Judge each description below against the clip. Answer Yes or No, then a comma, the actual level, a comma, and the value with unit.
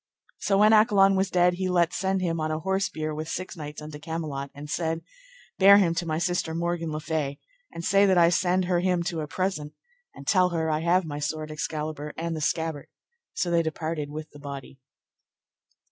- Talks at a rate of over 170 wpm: Yes, fast, 205 wpm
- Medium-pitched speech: Yes, medium, 165 Hz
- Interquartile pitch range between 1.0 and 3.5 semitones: Yes, average, 2.9 semitones